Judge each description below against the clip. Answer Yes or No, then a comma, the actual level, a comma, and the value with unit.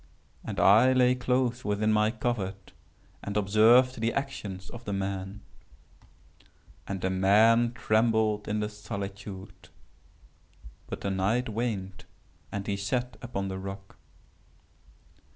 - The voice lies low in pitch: Yes, low, 105 Hz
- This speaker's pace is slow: Yes, slow, 115 wpm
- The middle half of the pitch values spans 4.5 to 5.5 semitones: No, average, 3.4 semitones